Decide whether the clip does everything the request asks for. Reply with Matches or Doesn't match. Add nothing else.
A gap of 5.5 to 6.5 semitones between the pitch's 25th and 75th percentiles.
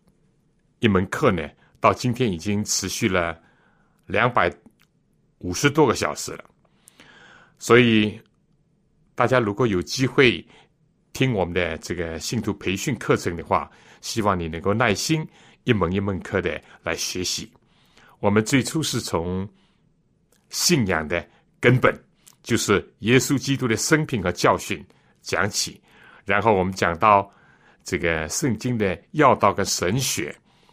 Matches